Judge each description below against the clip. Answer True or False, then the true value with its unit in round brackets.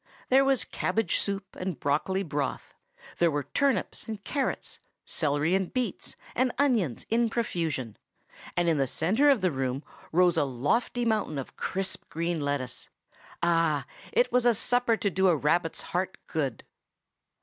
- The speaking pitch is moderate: True (180 Hz)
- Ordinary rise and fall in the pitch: False (7.5 semitones)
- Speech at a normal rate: True (155 wpm)